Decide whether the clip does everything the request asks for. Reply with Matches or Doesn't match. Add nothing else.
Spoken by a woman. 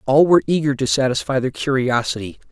Doesn't match